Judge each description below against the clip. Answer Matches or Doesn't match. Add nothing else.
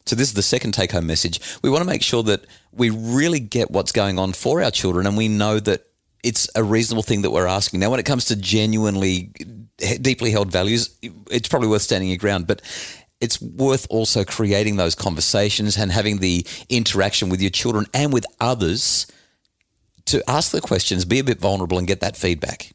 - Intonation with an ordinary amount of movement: Matches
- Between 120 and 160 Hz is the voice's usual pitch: Doesn't match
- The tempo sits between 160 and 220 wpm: Matches